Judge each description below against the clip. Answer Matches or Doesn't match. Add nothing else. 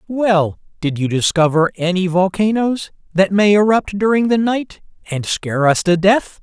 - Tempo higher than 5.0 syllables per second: Doesn't match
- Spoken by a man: Matches